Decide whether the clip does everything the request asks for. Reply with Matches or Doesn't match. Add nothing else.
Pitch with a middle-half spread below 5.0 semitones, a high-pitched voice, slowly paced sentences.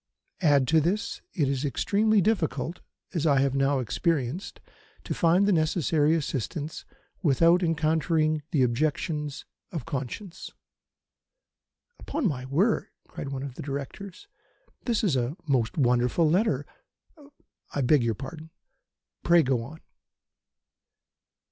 Doesn't match